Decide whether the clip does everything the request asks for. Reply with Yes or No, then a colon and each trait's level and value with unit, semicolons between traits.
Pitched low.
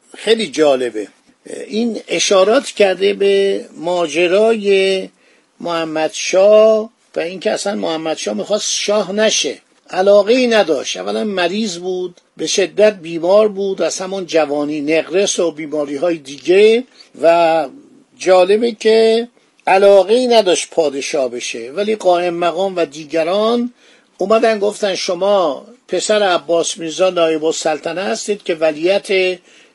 No: high, 190 Hz